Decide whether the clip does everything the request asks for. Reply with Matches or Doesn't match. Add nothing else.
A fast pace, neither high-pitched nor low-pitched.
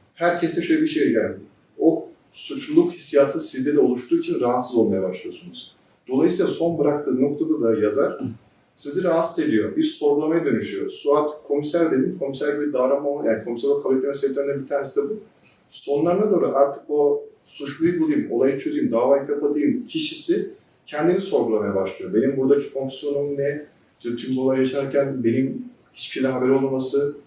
Matches